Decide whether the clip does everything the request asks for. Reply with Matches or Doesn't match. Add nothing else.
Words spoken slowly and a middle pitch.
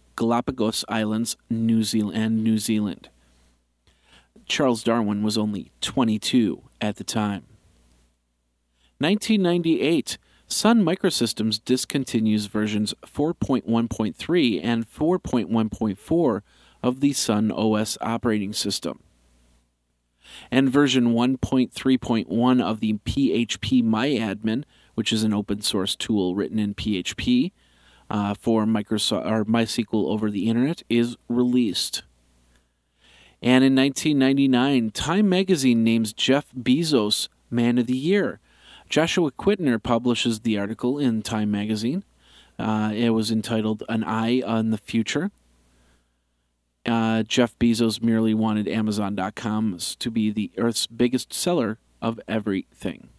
Doesn't match